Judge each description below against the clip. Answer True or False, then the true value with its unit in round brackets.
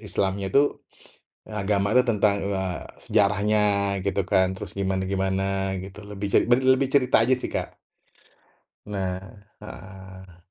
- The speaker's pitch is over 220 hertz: False (100 Hz)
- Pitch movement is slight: True (1.6 semitones)